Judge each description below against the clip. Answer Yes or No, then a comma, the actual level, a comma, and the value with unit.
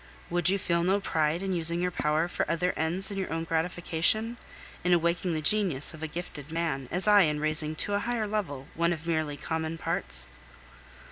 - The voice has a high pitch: No, medium, 170 Hz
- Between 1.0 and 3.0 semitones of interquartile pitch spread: Yes, average, 2.7 semitones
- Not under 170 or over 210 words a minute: Yes, average, 200 wpm